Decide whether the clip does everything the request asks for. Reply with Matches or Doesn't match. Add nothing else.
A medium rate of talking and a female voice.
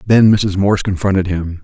Doesn't match